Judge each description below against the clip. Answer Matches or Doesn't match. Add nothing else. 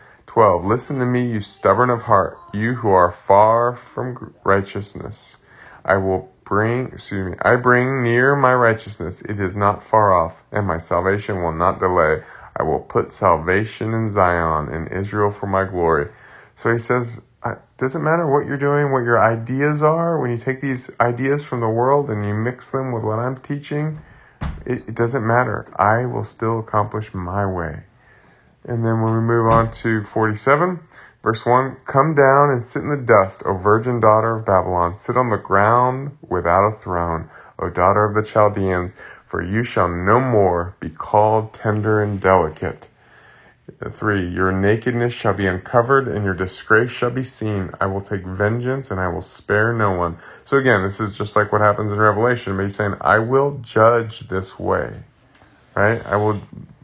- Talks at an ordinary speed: Matches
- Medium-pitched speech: Doesn't match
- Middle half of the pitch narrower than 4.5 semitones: Matches